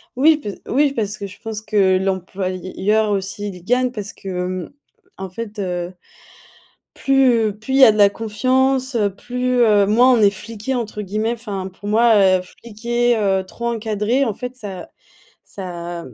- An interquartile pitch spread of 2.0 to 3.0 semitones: No, average, 3.7 semitones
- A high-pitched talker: Yes, high, 210 Hz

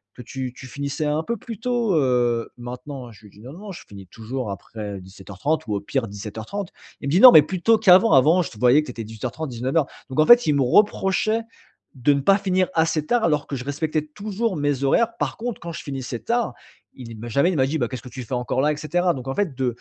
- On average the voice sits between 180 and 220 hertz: No, medium, 140 Hz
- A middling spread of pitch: No, wide, 6.7 semitones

